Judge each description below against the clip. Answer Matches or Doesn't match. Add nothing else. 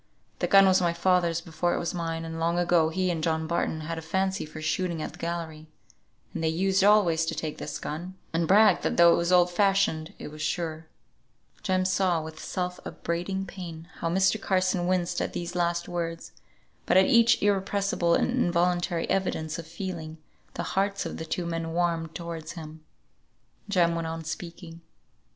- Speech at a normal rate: Matches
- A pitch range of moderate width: Doesn't match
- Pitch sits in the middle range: Matches